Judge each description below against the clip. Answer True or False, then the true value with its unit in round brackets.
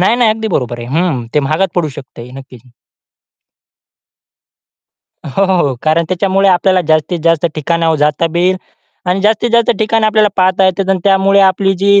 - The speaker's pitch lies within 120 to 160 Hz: False (185 Hz)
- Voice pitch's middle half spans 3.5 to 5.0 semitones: True (4.0 semitones)